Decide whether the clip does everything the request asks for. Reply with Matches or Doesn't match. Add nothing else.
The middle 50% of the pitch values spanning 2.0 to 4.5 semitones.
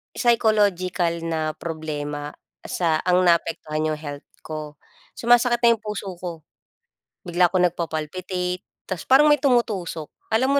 Doesn't match